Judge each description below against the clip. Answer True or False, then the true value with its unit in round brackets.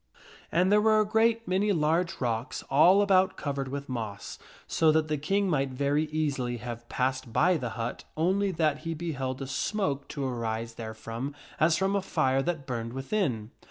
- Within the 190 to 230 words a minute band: False (180 wpm)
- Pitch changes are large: True (6.3 semitones)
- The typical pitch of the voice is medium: True (145 Hz)